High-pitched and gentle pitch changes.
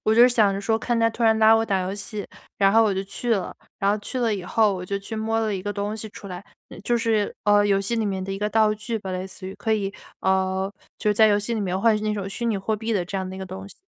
Yes: high, 205 Hz; narrow, 2.3 semitones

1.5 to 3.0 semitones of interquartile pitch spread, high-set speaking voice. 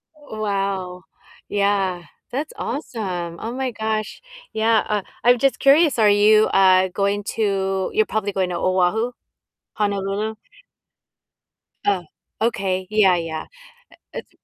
Yes: average, 2.7 semitones; high, 205 Hz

